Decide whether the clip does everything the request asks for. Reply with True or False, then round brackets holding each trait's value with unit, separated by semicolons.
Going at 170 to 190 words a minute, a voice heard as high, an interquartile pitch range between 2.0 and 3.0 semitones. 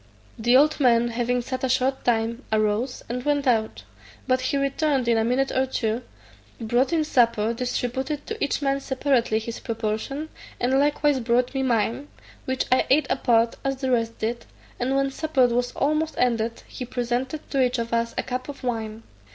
True (185 wpm; 250 Hz; 2.7 semitones)